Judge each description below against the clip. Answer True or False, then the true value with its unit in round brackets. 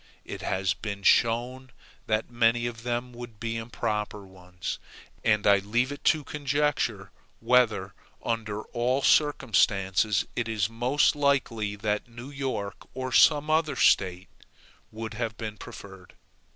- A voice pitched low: True (115 Hz)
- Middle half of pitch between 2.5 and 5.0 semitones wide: True (3.6 semitones)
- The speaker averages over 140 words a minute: False (135 wpm)